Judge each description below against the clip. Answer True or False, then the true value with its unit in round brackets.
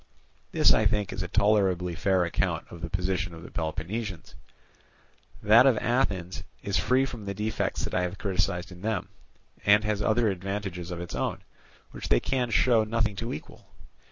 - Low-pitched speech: True (100 Hz)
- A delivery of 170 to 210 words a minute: True (180 wpm)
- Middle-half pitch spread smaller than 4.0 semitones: True (3.4 semitones)